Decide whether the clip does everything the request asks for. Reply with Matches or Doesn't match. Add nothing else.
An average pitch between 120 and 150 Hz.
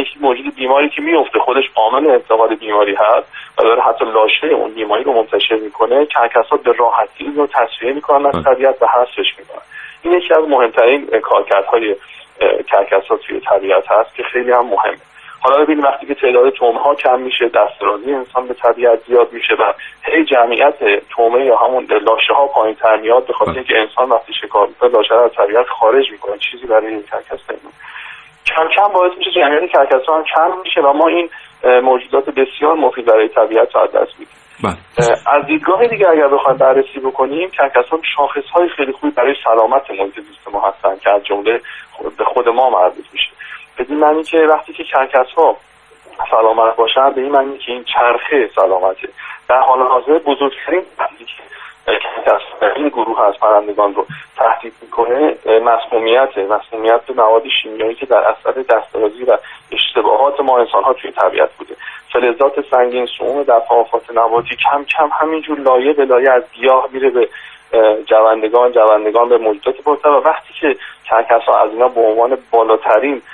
Matches